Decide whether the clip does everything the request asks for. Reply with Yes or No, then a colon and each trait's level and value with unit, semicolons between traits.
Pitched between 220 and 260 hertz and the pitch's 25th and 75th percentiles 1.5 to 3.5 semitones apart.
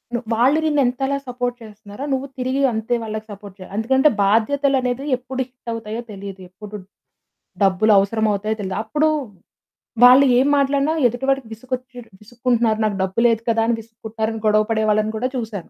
Yes: high, 230 Hz; average, 3.2 semitones